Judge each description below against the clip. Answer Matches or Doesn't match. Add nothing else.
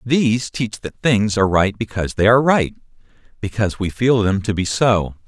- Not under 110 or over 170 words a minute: Doesn't match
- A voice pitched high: Doesn't match